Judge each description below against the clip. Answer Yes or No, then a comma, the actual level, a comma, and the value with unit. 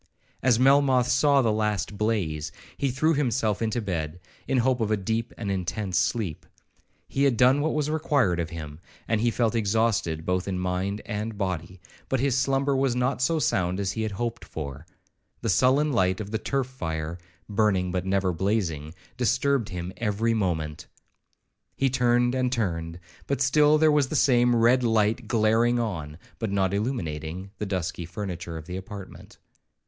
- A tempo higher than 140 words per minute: Yes, average, 170 wpm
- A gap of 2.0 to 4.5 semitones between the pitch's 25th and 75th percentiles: No, wide, 5.5 semitones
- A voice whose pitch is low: Yes, low, 110 Hz